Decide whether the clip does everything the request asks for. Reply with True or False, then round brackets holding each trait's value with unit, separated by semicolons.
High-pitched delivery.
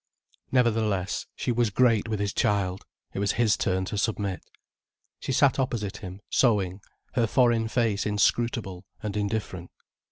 False (105 Hz)